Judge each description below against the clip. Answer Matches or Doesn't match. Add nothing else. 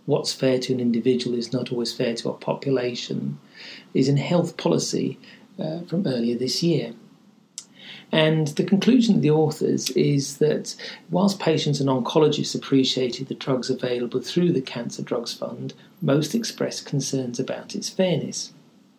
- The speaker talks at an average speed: Matches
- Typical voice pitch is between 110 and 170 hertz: Matches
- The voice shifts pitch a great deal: Matches